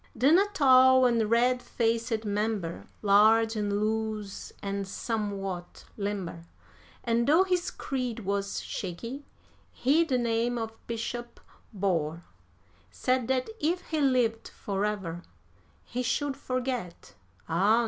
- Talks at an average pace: No, slow, 120 wpm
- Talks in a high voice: Yes, high, 225 Hz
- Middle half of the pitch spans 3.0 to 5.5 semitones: Yes, average, 4.0 semitones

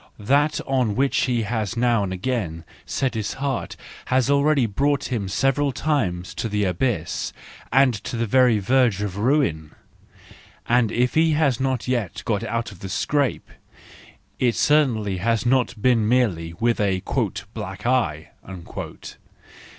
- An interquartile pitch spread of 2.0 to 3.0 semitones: No, average, 4.6 semitones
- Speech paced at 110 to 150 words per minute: Yes, average, 145 wpm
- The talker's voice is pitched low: Yes, low, 115 Hz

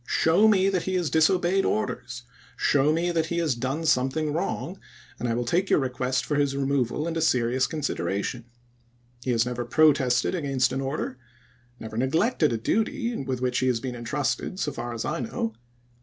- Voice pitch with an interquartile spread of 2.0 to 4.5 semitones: No, average, 5.0 semitones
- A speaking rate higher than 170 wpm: Yes, average, 190 wpm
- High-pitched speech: No, low, 135 Hz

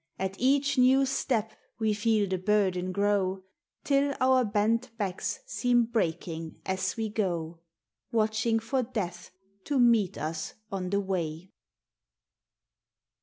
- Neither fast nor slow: No, slow, 125 wpm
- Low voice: No, high, 210 Hz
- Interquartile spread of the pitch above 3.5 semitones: Yes, average, 4.5 semitones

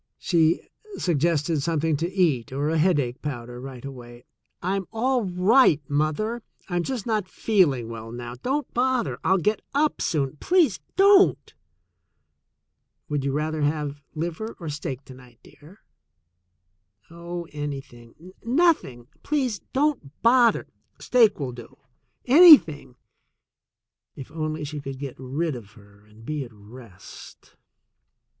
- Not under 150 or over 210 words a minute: No, average, 140 wpm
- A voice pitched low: No, medium, 155 Hz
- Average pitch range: No, wide, 7.6 semitones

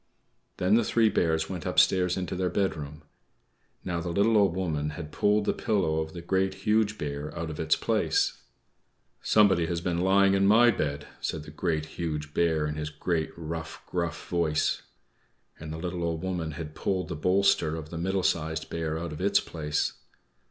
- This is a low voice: Yes, very low, 85 Hz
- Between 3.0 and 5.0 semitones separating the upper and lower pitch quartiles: Yes, average, 3.3 semitones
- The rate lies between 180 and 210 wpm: Yes, average, 185 wpm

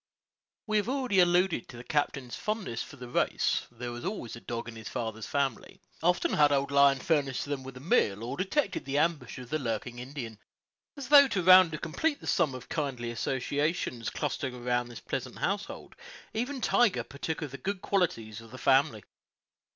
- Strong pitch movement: Yes, wide, 6.9 semitones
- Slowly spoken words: No, average, 190 wpm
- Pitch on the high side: No, medium, 140 Hz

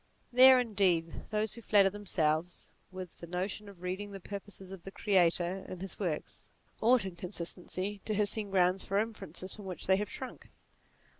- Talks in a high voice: Yes, high, 195 Hz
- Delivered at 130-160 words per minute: No, average, 175 wpm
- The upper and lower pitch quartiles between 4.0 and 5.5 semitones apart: No, narrow, 2.4 semitones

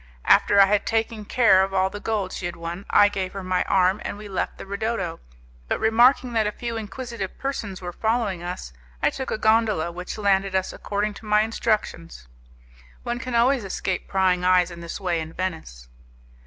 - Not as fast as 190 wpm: No, average, 195 wpm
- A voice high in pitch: Yes, high, 195 Hz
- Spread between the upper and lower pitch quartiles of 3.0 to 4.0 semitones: Yes, average, 3.3 semitones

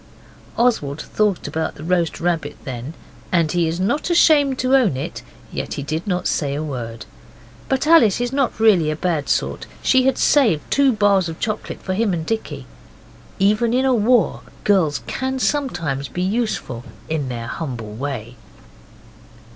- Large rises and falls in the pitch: Yes, wide, 8.4 semitones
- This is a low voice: No, medium, 180 Hz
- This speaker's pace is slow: No, average, 165 wpm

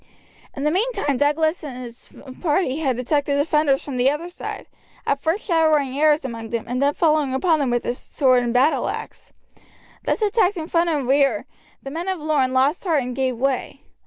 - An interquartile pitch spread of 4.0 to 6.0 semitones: No, average, 3.6 semitones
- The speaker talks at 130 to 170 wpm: No, average, 190 wpm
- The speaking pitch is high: Yes, very high, 285 Hz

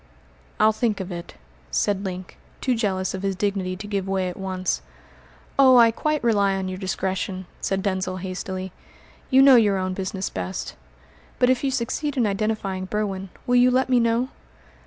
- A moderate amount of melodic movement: Yes, average, 3.8 semitones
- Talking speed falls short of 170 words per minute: No, average, 180 wpm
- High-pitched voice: Yes, high, 195 Hz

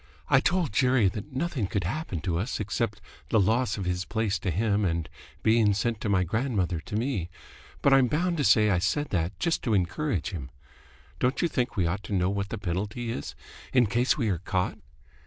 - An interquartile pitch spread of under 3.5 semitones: No, average, 4.9 semitones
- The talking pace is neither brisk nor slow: No, fast, 210 wpm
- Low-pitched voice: Yes, low, 105 Hz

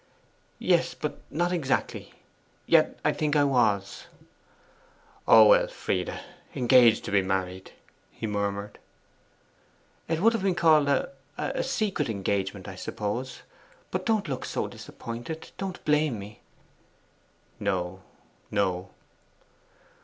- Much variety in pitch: Yes, wide, 8.3 semitones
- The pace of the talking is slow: Yes, slow, 110 wpm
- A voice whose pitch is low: Yes, low, 130 Hz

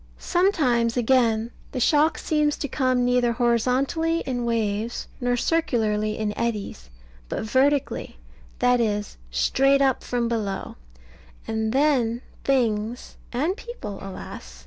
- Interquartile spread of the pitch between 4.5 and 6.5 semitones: No, average, 3.7 semitones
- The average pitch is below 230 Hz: No, high, 245 Hz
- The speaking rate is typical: No, slow, 120 wpm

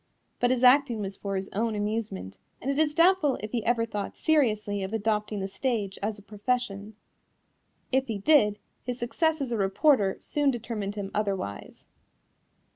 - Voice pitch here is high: Yes, high, 220 Hz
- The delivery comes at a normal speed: Yes, average, 170 wpm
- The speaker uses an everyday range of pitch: Yes, average, 4.1 semitones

